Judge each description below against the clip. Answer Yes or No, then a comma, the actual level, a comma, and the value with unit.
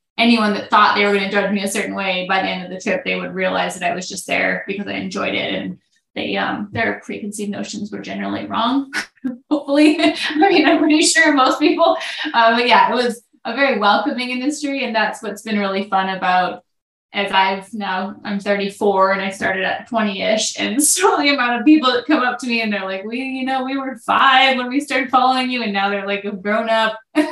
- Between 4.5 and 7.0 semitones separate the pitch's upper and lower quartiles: Yes, average, 5.2 semitones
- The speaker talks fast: Yes, fast, 235 wpm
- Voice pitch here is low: No, high, 225 Hz